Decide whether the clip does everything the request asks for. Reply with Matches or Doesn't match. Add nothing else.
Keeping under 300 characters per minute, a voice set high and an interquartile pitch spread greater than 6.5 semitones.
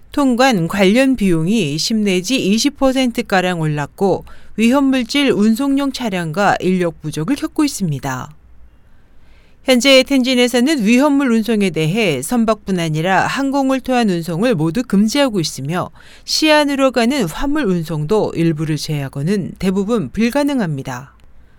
Matches